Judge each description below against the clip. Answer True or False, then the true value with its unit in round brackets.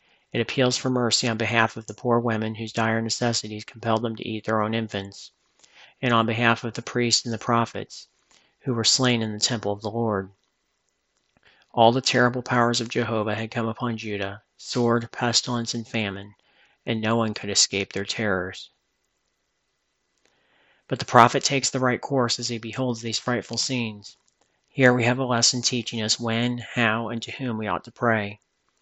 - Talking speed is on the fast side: False (185 wpm)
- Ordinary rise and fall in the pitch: False (1.8 semitones)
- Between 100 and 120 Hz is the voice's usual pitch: True (115 Hz)